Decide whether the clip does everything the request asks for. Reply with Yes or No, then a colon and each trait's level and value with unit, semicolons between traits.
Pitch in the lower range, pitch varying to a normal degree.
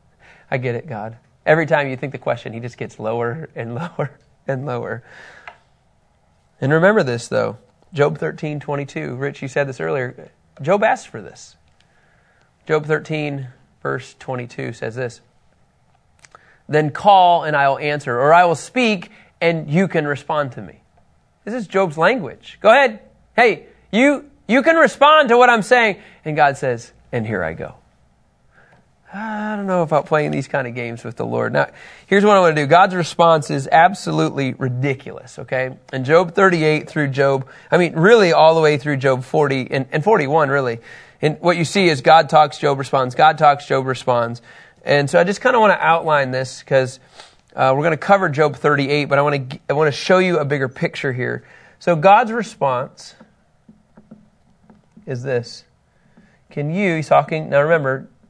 No: medium, 150 Hz; average, 4.5 semitones